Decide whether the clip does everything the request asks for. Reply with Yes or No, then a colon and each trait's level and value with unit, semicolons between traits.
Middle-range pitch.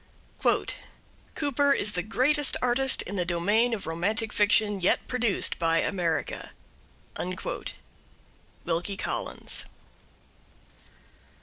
No: high, 205 Hz